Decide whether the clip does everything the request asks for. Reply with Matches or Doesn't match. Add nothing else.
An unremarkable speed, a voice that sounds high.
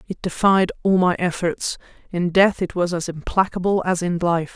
Doesn't match